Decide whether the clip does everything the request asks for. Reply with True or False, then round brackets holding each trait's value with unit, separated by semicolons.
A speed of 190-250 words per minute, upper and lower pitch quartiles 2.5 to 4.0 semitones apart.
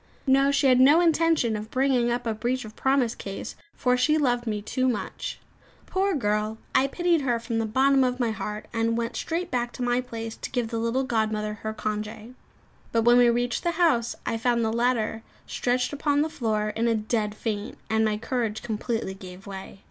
True (205 wpm; 3.0 semitones)